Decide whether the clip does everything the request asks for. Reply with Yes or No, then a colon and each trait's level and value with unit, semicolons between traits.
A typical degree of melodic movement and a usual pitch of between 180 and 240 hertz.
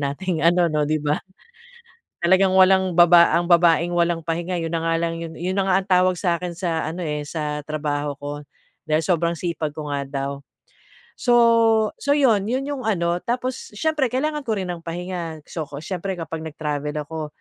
No: average, 3.4 semitones; medium, 170 Hz